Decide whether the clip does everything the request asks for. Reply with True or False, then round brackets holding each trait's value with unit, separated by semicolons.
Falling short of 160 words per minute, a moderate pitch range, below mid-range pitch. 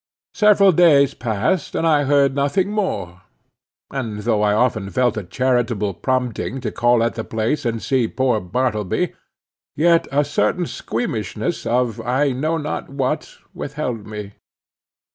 True (145 wpm; 4.8 semitones; 125 Hz)